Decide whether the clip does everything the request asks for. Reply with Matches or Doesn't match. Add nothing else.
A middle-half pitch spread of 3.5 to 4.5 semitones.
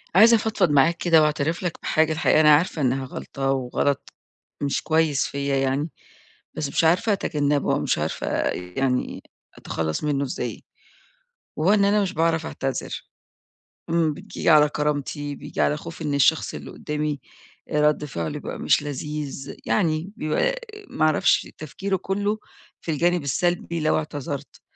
Doesn't match